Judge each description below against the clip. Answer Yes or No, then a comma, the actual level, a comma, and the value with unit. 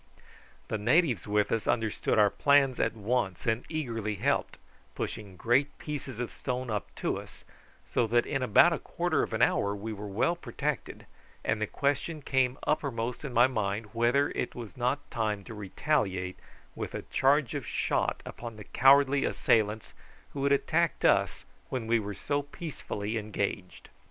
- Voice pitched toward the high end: No, low, 120 Hz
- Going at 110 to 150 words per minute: No, average, 165 wpm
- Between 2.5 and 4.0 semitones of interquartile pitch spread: No, average, 4.8 semitones